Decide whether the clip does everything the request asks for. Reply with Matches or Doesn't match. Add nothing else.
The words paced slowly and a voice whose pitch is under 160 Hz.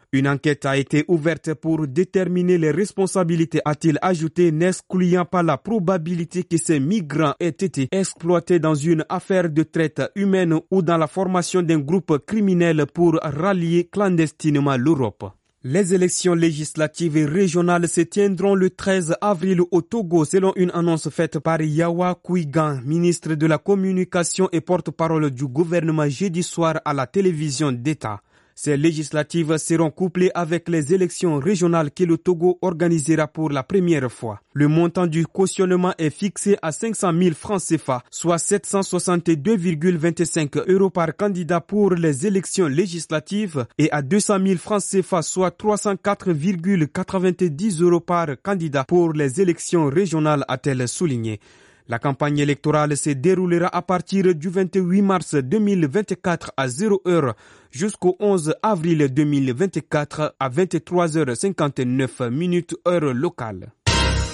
Doesn't match